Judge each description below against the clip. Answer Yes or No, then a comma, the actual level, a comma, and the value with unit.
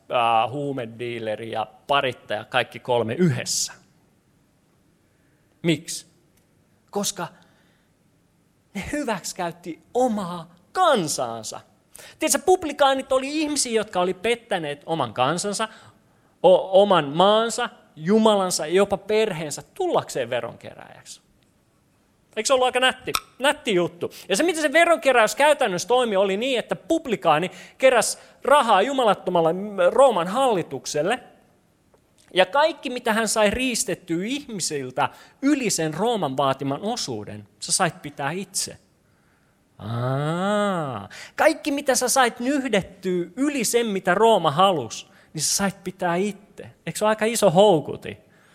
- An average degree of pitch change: No, wide, 7.0 semitones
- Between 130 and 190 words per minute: No, average, 115 wpm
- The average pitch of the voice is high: Yes, high, 195 Hz